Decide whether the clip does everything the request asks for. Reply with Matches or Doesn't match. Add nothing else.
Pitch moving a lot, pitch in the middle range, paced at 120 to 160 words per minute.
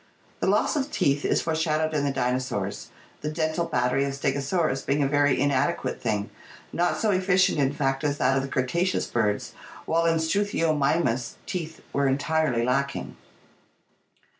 Doesn't match